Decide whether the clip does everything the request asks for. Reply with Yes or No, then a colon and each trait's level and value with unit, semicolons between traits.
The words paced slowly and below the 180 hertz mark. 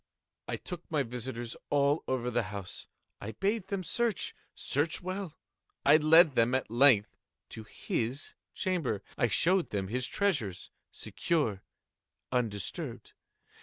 Yes: slow, 125 wpm; low, 135 Hz